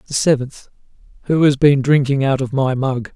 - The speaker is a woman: No, male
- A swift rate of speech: No, average, 190 wpm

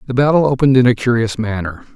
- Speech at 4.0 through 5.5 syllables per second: No, 7.1 syllables/s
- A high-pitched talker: No, low, 125 Hz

